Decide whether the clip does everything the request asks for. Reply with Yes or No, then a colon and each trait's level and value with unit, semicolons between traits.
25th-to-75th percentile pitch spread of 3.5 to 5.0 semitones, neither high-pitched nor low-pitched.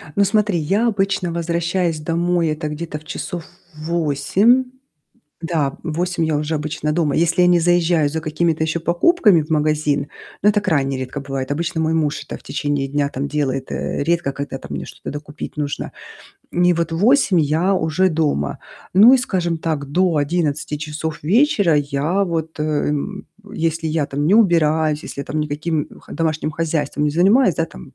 No: average, 2.8 semitones; medium, 160 Hz